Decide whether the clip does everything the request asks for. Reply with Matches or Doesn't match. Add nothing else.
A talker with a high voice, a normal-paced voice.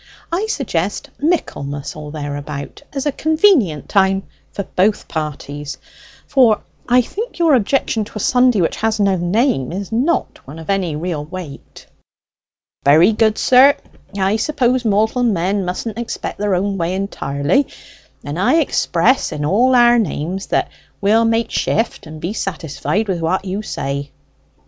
Matches